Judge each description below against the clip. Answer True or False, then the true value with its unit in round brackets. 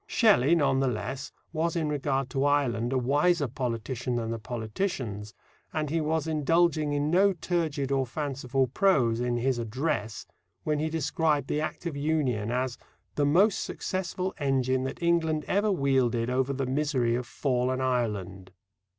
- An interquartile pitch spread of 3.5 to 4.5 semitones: True (4.2 semitones)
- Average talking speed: True (160 wpm)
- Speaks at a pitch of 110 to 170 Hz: True (135 Hz)